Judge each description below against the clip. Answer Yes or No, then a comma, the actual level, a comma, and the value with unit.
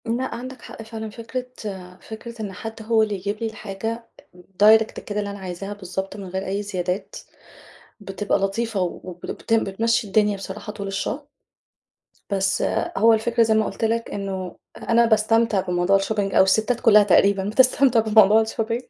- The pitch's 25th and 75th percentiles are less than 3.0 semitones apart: Yes, narrow, 2.6 semitones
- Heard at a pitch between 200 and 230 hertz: Yes, high, 215 Hz